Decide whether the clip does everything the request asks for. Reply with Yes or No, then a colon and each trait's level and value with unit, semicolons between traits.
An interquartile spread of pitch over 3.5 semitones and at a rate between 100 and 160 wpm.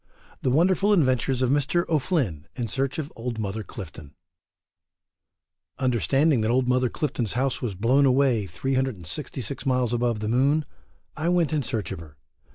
Yes: average, 4.0 semitones; average, 155 wpm